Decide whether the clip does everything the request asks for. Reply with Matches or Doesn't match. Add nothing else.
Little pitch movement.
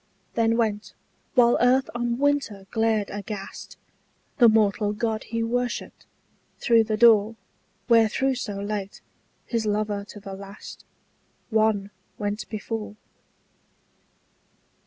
Matches